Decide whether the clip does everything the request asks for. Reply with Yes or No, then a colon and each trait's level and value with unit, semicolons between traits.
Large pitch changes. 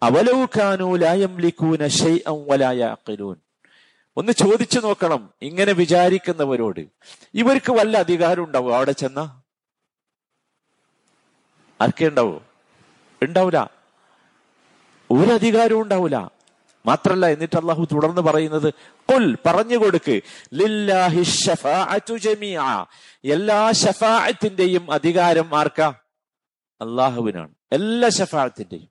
Yes: wide, 5.8 semitones